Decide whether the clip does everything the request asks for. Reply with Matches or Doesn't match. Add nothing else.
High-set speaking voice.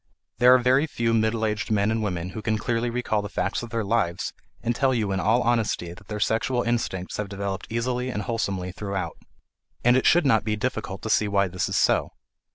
Doesn't match